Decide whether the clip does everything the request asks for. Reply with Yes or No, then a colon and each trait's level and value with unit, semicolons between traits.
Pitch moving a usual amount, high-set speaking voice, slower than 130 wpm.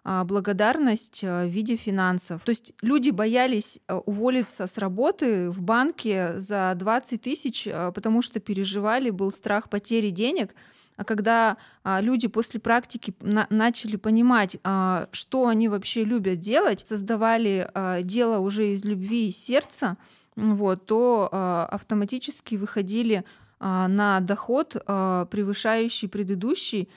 Yes: average, 3.0 semitones; high, 215 Hz; average, 115 wpm